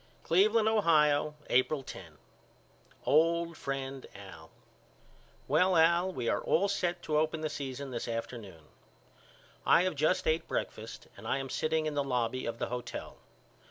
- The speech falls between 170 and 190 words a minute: No, average, 150 wpm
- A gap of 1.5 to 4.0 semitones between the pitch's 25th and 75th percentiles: No, average, 4.7 semitones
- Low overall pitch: No, medium, 150 Hz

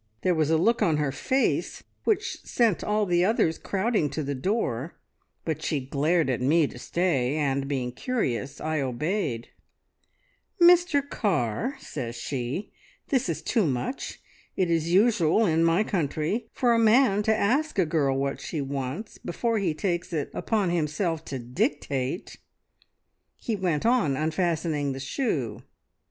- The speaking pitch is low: No, medium, 165 Hz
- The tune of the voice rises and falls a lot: Yes, wide, 7.2 semitones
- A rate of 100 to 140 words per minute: No, average, 150 wpm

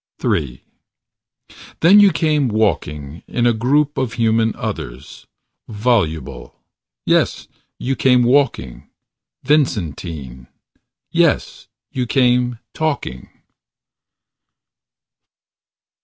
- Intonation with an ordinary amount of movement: No, wide, 9.0 semitones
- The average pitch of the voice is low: Yes, low, 120 Hz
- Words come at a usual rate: No, slow, 80 wpm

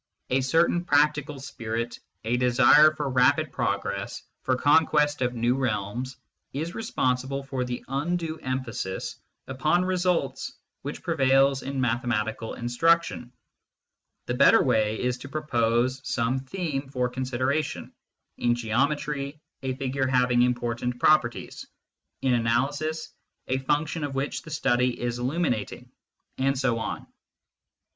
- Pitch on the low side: Yes, low, 130 Hz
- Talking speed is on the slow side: Yes, slow, 120 wpm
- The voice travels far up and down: No, average, 3.2 semitones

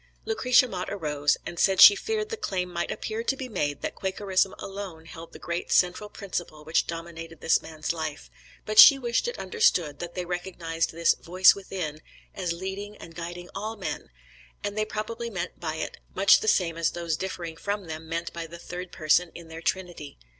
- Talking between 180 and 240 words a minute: Yes, average, 195 wpm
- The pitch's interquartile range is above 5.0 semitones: No, average, 3.5 semitones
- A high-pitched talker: No, medium, 180 Hz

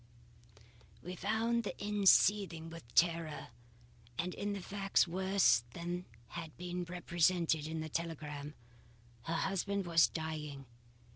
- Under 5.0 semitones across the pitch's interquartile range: Yes, average, 3.2 semitones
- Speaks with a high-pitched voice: No, medium, 170 Hz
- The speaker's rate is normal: No, slow, 120 wpm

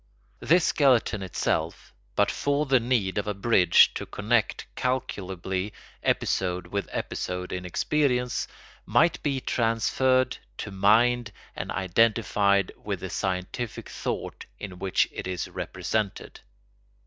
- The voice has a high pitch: No, low, 105 Hz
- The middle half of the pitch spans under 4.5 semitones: No, average, 5.0 semitones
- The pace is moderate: No, slow, 120 wpm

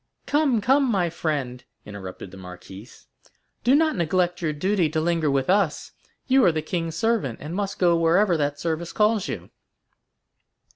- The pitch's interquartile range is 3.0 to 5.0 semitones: No, wide, 5.6 semitones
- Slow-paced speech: No, average, 160 wpm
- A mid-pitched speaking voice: Yes, medium, 170 Hz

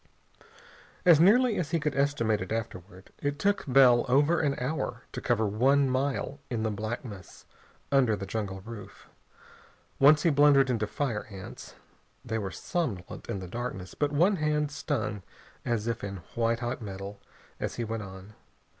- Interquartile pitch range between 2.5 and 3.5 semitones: No, average, 5.3 semitones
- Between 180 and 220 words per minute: No, average, 165 wpm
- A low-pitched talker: Yes, low, 120 Hz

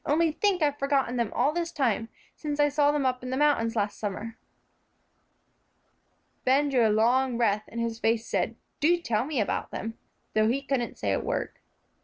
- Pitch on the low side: No, very high, 255 Hz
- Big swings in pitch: No, average, 4.3 semitones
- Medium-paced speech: Yes, average, 190 wpm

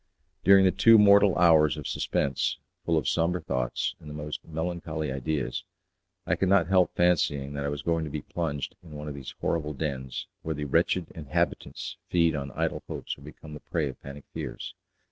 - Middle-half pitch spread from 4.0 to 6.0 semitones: No, average, 3.3 semitones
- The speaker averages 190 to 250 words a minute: Yes, average, 195 wpm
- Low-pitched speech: Yes, very low, 75 Hz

